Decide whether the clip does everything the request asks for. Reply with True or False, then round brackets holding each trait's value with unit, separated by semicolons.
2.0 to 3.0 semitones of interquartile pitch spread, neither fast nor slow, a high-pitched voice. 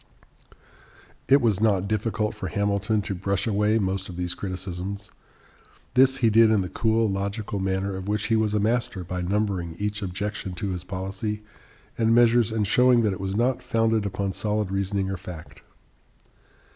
False (2.6 semitones; 170 wpm; 100 Hz)